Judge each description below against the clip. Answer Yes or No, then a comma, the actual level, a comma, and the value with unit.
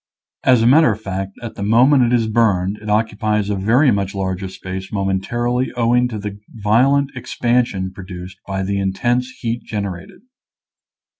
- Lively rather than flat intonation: No, average, 3.8 semitones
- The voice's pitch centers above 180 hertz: No, low, 105 Hz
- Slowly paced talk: No, average, 165 wpm